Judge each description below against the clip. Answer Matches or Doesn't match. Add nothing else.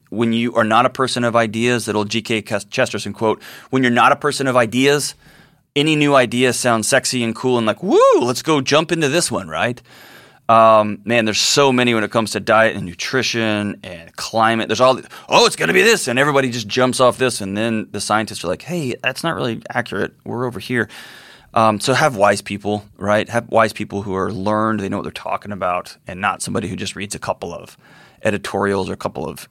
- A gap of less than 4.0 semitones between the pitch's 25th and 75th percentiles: Matches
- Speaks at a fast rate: Matches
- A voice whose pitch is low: Matches